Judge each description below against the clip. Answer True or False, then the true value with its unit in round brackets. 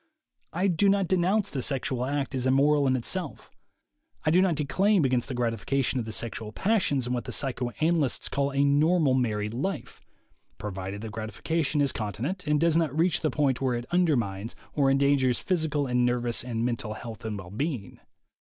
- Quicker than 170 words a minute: True (185 wpm)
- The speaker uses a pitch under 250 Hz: True (135 Hz)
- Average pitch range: True (5.0 semitones)